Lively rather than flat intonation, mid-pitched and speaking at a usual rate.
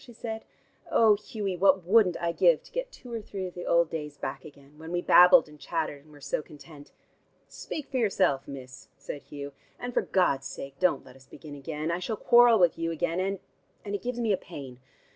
No: wide, 6.1 semitones; medium, 175 Hz; fast, 220 wpm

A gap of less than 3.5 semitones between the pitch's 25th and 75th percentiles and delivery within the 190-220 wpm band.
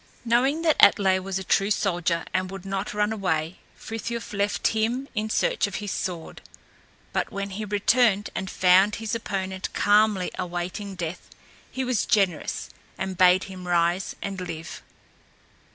No: average, 2.8 semitones; average, 150 wpm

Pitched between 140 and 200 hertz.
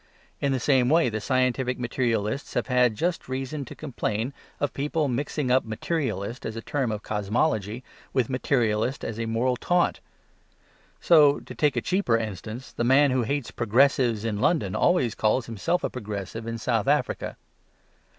No: low, 125 Hz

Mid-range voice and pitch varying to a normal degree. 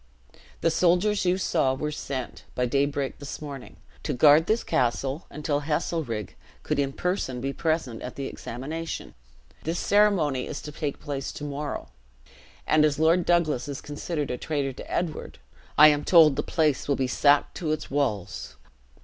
Yes: medium, 150 Hz; average, 3.0 semitones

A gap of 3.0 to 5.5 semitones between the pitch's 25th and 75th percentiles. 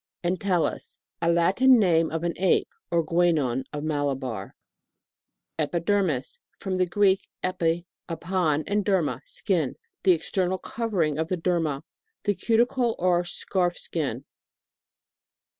Yes: average, 3.3 semitones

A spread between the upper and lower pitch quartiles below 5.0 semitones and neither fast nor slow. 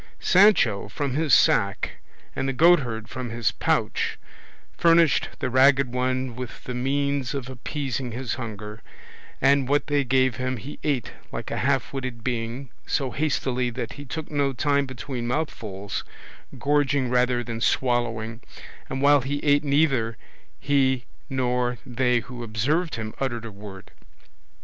Yes: average, 2.9 semitones; average, 145 wpm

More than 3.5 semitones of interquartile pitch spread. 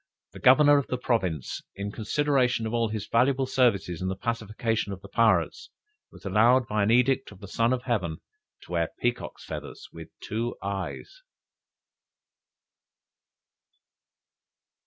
Yes: average, 4.2 semitones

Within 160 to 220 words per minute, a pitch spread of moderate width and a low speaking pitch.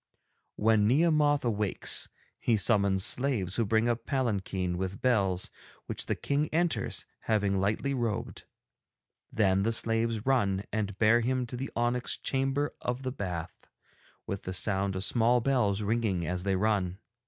No: average, 150 wpm; average, 4.2 semitones; low, 110 Hz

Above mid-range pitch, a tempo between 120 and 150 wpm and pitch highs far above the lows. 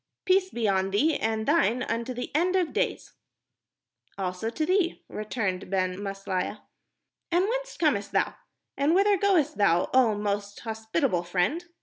Yes: high, 225 Hz; average, 145 wpm; wide, 8.9 semitones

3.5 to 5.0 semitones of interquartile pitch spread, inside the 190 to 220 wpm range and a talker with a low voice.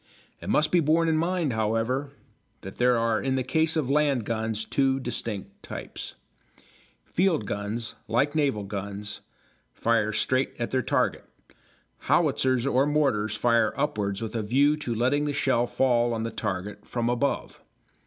No: average, 4.3 semitones; average, 155 wpm; low, 120 Hz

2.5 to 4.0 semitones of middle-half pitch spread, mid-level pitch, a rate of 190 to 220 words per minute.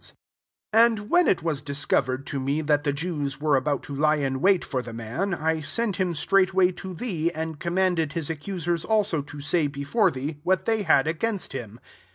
No: average, 4.7 semitones; medium, 160 Hz; average, 200 wpm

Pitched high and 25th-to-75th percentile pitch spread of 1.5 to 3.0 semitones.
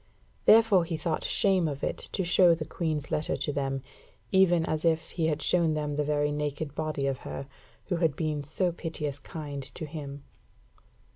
No: medium, 155 Hz; narrow, 2.5 semitones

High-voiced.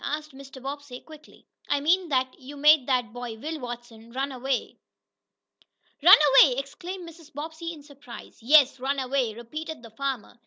Yes: very high, 275 Hz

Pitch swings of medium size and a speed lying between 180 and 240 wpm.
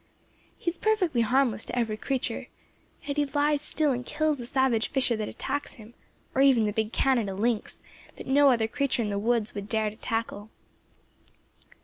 Yes: average, 4.3 semitones; average, 185 wpm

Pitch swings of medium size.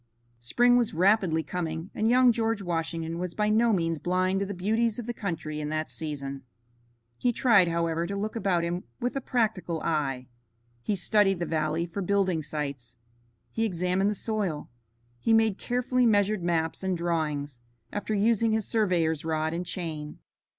Yes: average, 5.0 semitones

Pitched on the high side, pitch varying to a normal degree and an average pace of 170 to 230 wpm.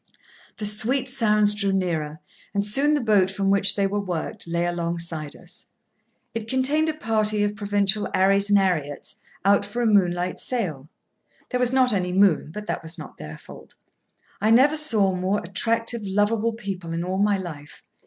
Yes: high, 200 Hz; average, 3.6 semitones; average, 175 wpm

